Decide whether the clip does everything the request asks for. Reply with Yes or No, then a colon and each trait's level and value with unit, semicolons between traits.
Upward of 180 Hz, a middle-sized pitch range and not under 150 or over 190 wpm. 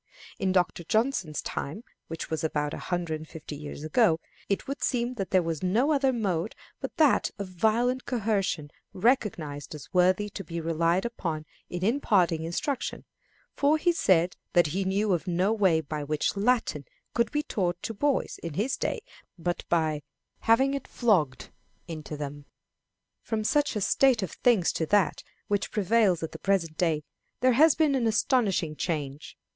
No: high, 190 Hz; wide, 6.3 semitones; average, 170 wpm